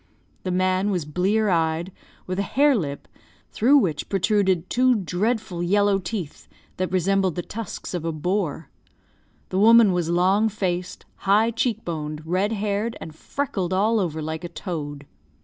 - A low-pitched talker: No, medium, 185 Hz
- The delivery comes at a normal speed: Yes, average, 155 wpm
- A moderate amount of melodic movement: Yes, average, 3.6 semitones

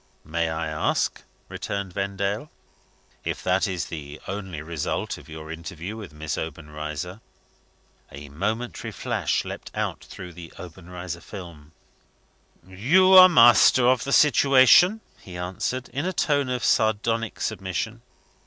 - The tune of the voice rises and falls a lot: Yes, wide, 6.4 semitones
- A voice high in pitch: No, very low, 95 Hz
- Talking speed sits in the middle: No, slow, 130 wpm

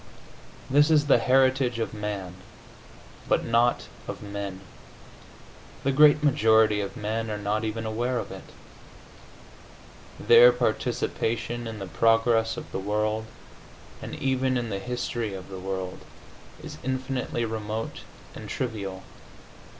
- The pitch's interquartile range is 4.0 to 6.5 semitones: No, average, 2.9 semitones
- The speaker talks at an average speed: No, slow, 125 wpm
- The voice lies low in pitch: Yes, low, 115 Hz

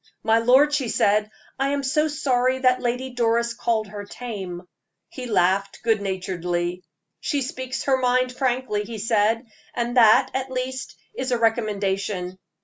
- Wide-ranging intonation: No, average, 4.0 semitones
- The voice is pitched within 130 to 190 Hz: No, high, 235 Hz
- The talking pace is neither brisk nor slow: Yes, average, 150 wpm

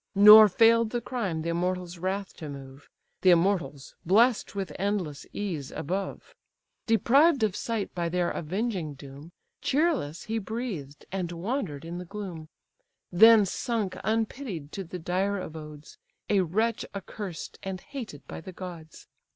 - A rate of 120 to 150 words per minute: Yes, average, 145 wpm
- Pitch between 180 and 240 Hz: Yes, medium, 185 Hz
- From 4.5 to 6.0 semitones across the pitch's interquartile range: Yes, average, 4.8 semitones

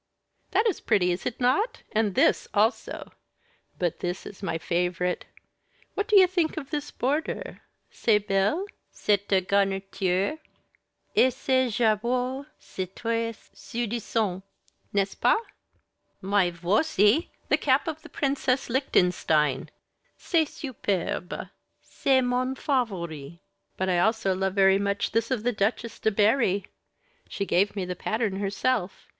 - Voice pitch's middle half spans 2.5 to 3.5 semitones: No, average, 5.2 semitones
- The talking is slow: Yes, slow, 130 wpm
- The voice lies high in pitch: Yes, high, 210 Hz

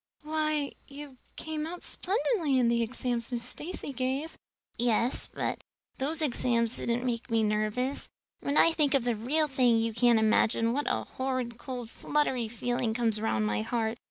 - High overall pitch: Yes, high, 245 Hz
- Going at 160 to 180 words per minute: Yes, average, 165 wpm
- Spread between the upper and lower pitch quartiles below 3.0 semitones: No, average, 3.7 semitones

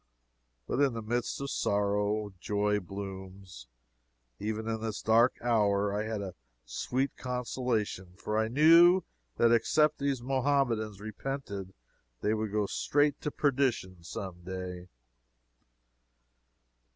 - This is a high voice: No, low, 110 Hz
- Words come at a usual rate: No, slow, 120 wpm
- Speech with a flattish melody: No, average, 4.2 semitones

